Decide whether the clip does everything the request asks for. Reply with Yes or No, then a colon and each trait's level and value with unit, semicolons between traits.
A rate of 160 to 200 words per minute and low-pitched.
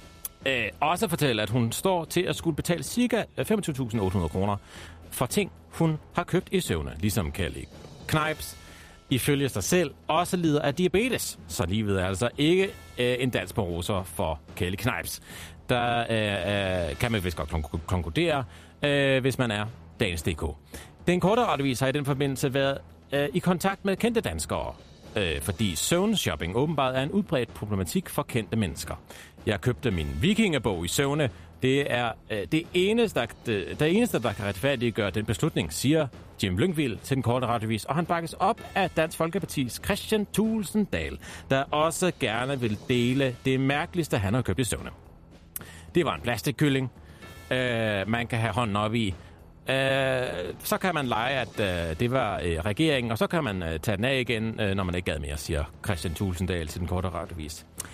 Yes: average, 170 wpm; low, 120 Hz